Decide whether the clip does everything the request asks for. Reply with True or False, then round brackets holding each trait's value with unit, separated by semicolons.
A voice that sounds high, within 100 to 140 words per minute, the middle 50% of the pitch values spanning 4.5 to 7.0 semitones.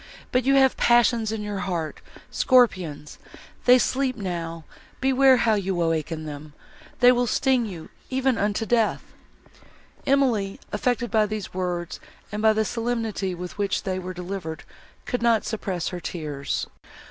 True (210 Hz; 135 wpm; 5.4 semitones)